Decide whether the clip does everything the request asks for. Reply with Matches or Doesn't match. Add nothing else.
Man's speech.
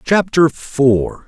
Matches